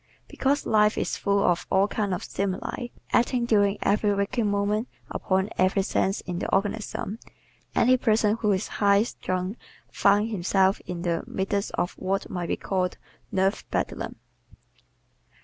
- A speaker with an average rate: Yes, average, 150 wpm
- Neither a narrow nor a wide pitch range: No, narrow, 2.1 semitones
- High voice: Yes, high, 200 Hz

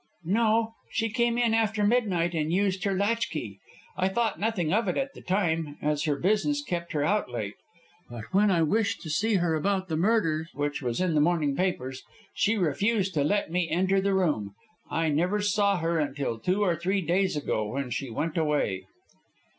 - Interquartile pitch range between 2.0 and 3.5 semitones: No, average, 5.3 semitones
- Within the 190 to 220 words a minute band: Yes, average, 195 wpm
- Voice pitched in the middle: Yes, medium, 180 Hz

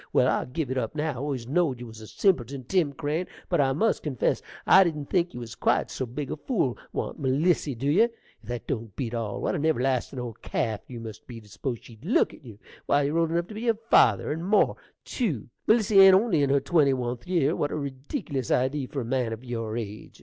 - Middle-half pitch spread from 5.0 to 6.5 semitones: Yes, average, 5.3 semitones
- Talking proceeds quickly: Yes, fast, 240 wpm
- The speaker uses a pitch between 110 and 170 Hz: Yes, low, 135 Hz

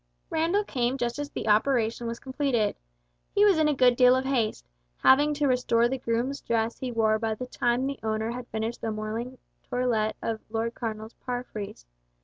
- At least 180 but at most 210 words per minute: Yes, average, 190 wpm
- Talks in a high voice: Yes, high, 240 Hz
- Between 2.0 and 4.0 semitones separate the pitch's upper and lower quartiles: Yes, average, 2.9 semitones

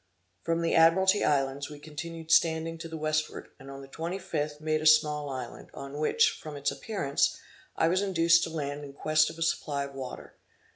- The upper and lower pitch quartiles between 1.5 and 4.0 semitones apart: Yes, narrow, 2.5 semitones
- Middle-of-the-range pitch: Yes, medium, 155 Hz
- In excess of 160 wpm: Yes, average, 200 wpm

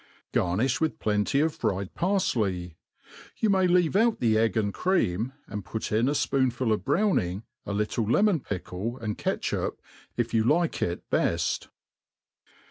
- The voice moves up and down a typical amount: No, wide, 7.7 semitones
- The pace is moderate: Yes, average, 155 wpm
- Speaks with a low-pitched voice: Yes, low, 115 Hz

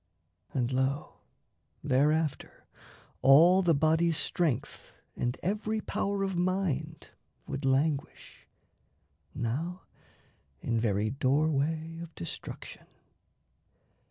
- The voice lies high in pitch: No, medium, 155 Hz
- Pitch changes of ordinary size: Yes, average, 4.3 semitones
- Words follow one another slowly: Yes, slow, 85 wpm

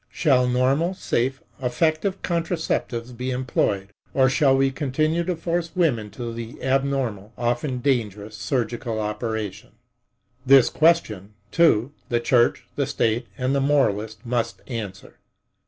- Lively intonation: No, average, 3.8 semitones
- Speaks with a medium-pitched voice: No, low, 125 Hz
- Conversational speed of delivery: No, slow, 125 wpm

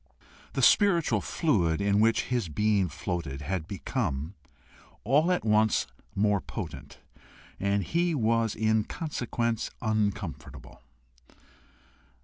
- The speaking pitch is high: No, low, 105 Hz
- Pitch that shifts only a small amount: No, average, 3.7 semitones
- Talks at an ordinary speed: No, slow, 105 wpm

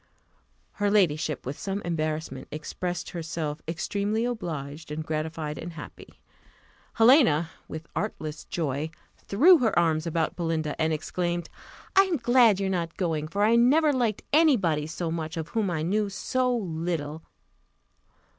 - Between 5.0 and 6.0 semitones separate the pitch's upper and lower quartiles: Yes, average, 5.3 semitones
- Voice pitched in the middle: Yes, medium, 170 Hz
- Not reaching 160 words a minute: Yes, average, 145 wpm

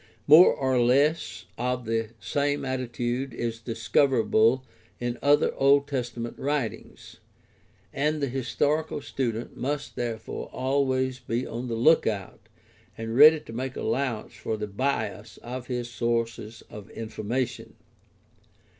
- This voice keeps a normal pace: No, slow, 120 wpm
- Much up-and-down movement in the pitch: No, average, 3.1 semitones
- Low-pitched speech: Yes, low, 125 Hz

